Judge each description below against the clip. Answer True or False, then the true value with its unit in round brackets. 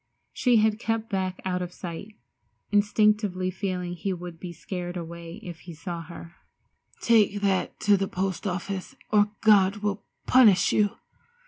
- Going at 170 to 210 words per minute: False (150 wpm)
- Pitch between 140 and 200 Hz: True (190 Hz)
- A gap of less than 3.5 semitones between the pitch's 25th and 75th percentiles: True (2.8 semitones)